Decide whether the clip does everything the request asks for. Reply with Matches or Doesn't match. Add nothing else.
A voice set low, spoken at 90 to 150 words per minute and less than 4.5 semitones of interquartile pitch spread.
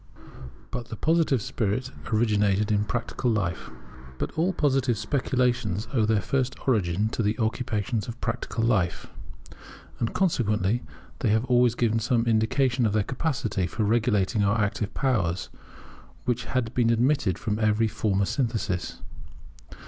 Matches